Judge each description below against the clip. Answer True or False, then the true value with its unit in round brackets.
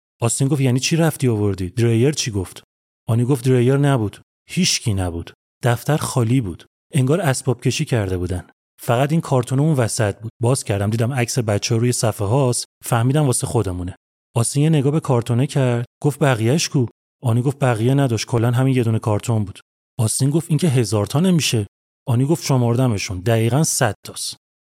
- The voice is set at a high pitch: False (125 Hz)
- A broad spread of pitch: False (3.6 semitones)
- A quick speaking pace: True (170 wpm)